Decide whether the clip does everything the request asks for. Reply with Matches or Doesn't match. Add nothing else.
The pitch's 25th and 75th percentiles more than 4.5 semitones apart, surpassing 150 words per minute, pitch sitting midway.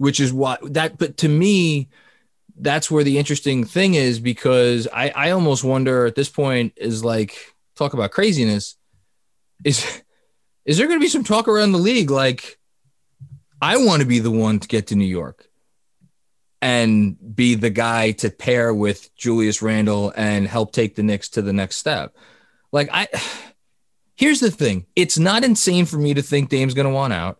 Doesn't match